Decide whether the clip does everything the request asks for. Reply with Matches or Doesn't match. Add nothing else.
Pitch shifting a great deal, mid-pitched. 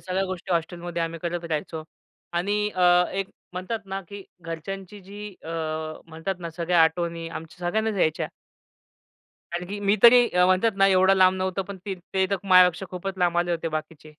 Doesn't match